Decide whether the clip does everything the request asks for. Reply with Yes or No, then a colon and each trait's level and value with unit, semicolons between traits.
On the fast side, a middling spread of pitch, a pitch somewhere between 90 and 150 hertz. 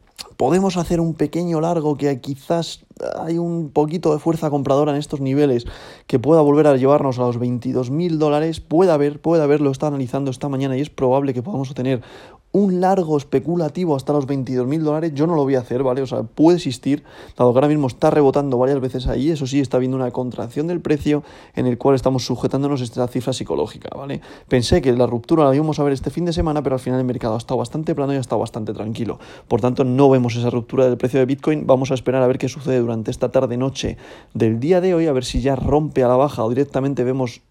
Yes: fast, 235 wpm; average, 3.0 semitones; low, 135 Hz